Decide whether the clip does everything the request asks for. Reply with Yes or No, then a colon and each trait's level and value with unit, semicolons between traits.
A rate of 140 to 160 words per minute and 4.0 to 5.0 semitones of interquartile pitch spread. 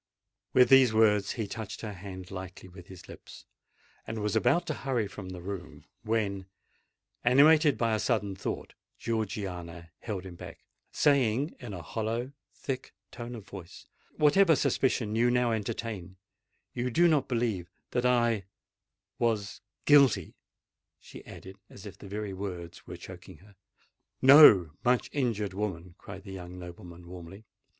Yes: average, 145 wpm; average, 4.5 semitones